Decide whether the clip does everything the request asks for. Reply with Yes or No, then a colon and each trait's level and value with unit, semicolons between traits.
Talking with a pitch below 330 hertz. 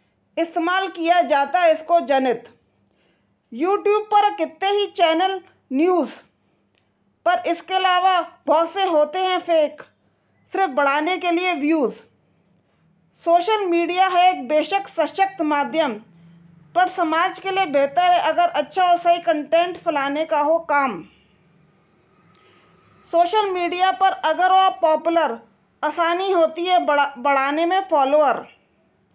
No: very high, 335 Hz